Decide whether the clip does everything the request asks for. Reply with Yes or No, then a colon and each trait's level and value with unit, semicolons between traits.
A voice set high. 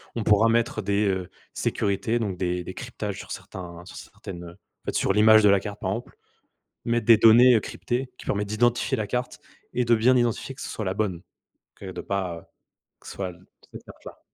No: low, 105 Hz